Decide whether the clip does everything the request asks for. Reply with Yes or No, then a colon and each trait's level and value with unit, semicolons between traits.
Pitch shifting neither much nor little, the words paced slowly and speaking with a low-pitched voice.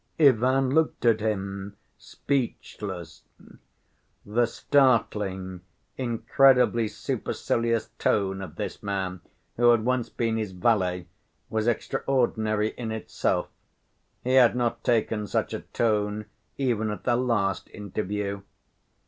Yes: average, 3.1 semitones; slow, 110 wpm; low, 110 Hz